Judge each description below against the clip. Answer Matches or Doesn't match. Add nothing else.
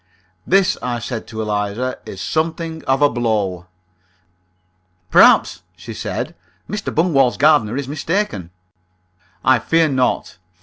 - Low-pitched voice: Matches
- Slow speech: Matches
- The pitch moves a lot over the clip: Matches